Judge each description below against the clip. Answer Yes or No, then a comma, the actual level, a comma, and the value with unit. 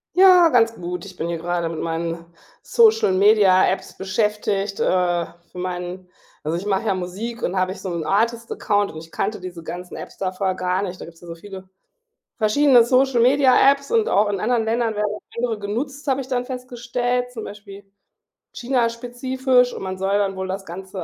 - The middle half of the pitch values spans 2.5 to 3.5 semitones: No, average, 4.9 semitones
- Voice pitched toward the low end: No, high, 205 Hz